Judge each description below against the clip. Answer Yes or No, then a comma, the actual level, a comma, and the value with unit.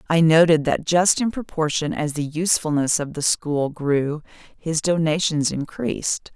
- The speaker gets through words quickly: No, average, 150 wpm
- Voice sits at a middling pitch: Yes, medium, 160 Hz